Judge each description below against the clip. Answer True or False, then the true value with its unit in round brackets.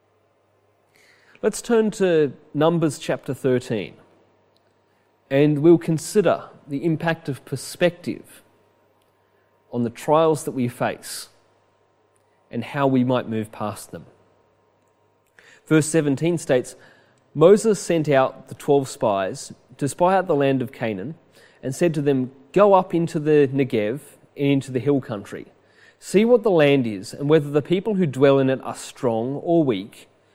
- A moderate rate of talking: True (145 wpm)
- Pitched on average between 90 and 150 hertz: True (140 Hz)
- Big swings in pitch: True (5.7 semitones)